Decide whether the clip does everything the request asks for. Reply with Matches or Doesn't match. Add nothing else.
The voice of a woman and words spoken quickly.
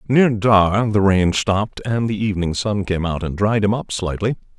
Doesn't match